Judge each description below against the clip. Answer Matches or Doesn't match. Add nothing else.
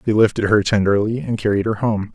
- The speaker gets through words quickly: Matches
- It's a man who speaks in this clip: Matches